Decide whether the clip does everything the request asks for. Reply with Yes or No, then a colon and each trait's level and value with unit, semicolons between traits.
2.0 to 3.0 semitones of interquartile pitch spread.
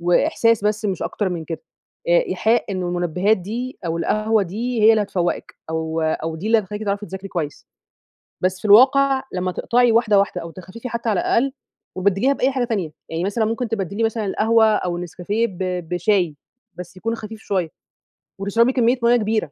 No: average, 4.2 semitones